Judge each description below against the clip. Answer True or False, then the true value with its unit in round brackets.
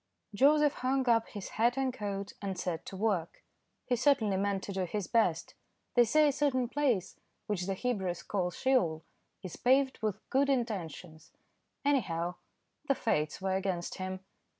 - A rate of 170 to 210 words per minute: False (160 wpm)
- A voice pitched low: False (205 Hz)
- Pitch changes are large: True (5.7 semitones)